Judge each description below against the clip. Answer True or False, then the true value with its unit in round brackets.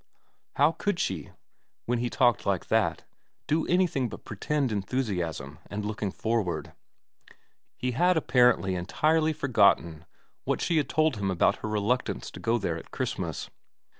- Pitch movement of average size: False (7.1 semitones)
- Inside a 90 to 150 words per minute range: True (145 wpm)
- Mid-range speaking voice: False (115 Hz)